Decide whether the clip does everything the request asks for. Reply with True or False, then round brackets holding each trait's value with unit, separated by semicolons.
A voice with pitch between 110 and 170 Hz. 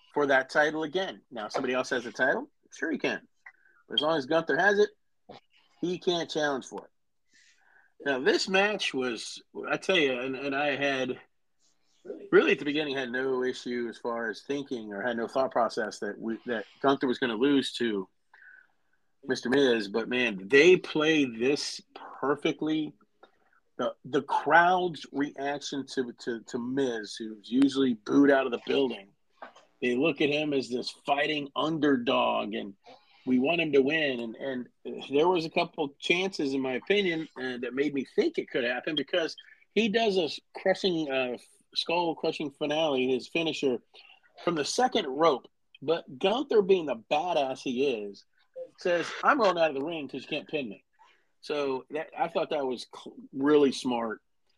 True (140 Hz)